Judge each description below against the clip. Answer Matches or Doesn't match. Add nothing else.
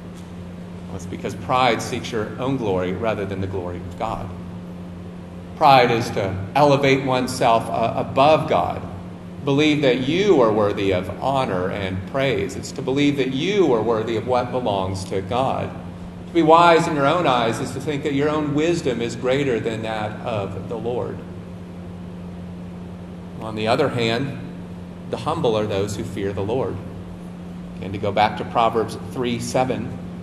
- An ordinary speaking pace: Matches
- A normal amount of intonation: Doesn't match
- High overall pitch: Doesn't match